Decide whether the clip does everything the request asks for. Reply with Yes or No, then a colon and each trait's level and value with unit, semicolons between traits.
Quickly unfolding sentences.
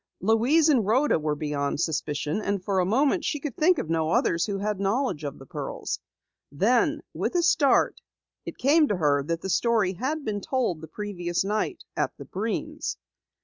No: average, 190 wpm